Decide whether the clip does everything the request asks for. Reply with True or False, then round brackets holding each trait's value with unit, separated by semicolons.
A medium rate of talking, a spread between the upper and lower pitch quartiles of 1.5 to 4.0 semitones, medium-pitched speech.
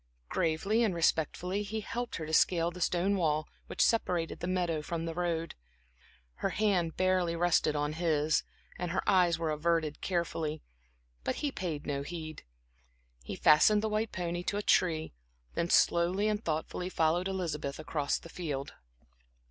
True (160 wpm; 2.9 semitones; 170 Hz)